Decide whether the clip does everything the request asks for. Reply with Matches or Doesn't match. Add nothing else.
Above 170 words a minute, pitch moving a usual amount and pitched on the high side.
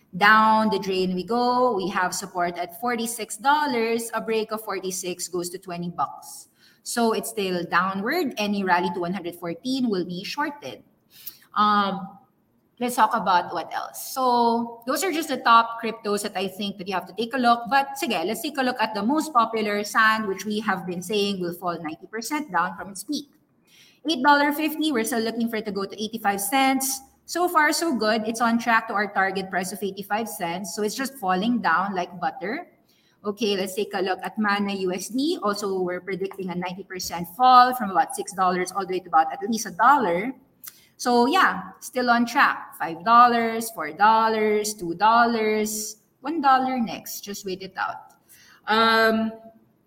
Matches